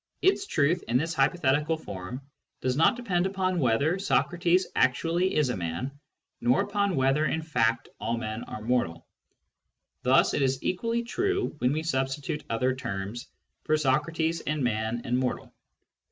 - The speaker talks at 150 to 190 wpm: Yes, average, 155 wpm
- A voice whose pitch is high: No, medium, 140 Hz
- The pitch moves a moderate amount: No, wide, 5.9 semitones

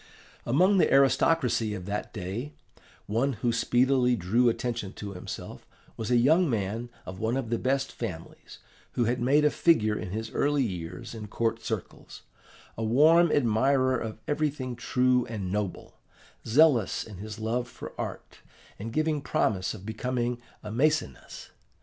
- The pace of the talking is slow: No, average, 155 wpm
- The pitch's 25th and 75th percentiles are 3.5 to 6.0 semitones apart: Yes, average, 3.8 semitones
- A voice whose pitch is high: No, low, 120 Hz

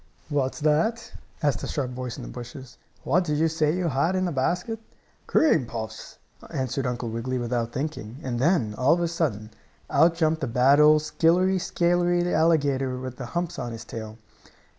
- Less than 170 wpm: No, average, 185 wpm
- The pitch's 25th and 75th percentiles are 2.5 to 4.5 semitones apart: No, average, 5.2 semitones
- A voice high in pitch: No, medium, 145 Hz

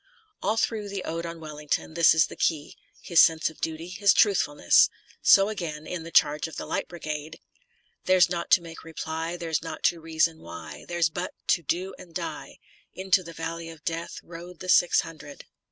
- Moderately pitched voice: Yes, medium, 165 Hz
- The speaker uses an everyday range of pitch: No, narrow, 1.9 semitones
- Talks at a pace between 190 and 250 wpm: Yes, average, 200 wpm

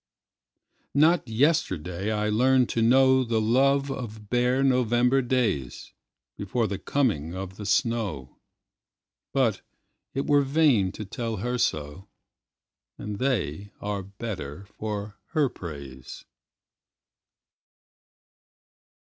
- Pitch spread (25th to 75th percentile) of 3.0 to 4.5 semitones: No, average, 4.9 semitones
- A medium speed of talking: No, slow, 90 wpm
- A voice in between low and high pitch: No, low, 110 Hz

